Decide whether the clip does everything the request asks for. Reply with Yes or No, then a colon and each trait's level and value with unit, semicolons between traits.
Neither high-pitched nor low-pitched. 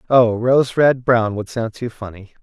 No: low, 115 Hz